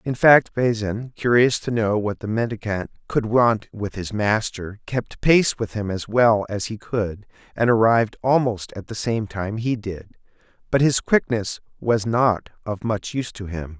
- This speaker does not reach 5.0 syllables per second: Yes, 4.3 syllables/s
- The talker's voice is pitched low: Yes, low, 110 Hz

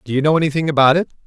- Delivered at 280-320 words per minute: Yes, fast, 285 wpm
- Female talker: No, male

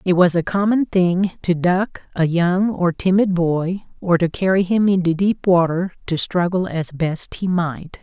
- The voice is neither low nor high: Yes, medium, 180 Hz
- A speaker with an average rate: Yes, average, 185 wpm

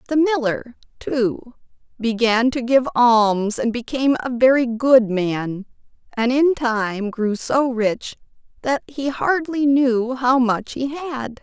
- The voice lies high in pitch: Yes, high, 245 Hz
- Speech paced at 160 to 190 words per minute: No, average, 140 wpm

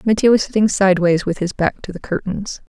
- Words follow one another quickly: Yes, fast, 220 wpm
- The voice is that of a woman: Yes, female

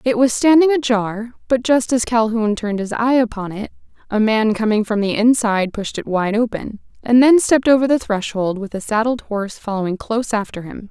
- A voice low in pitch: No, high, 225 Hz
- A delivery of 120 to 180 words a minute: No, fast, 205 wpm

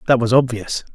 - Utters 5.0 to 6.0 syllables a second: Yes, 5.6 syllables/s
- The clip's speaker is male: Yes, male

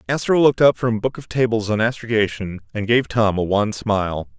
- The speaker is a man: Yes, male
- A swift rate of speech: Yes, fast, 220 wpm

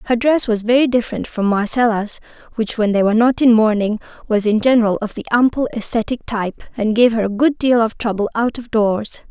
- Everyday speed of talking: No, fast, 215 wpm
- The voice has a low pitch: No, high, 225 Hz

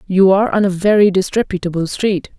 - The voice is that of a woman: Yes, female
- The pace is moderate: Yes, average, 175 wpm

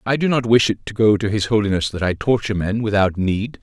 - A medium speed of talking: No, fast, 265 wpm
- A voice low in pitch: Yes, low, 105 Hz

